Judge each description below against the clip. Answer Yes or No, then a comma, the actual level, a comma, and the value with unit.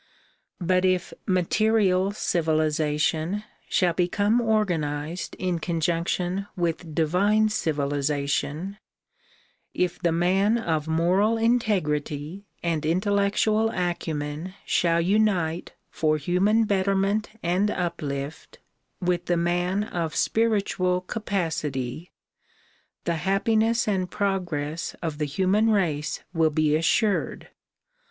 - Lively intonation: No, average, 4.0 semitones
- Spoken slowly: Yes, slow, 100 wpm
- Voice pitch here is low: No, medium, 180 Hz